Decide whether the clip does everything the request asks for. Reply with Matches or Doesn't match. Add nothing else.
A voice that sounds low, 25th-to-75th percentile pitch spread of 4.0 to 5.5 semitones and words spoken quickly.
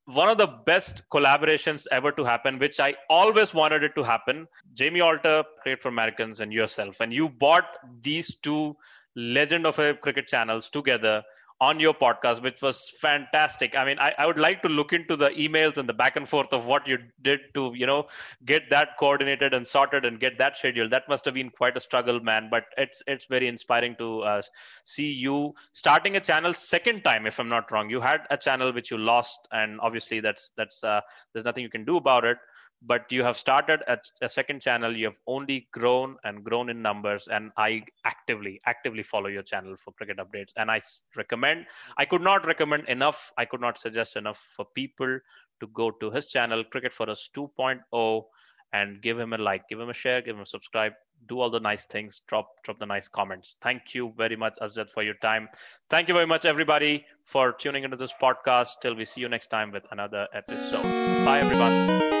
Matches